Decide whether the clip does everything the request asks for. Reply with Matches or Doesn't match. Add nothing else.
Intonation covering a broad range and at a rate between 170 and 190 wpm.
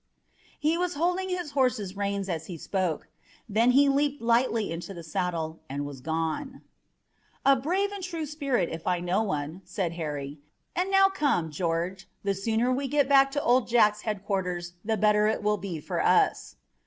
Matches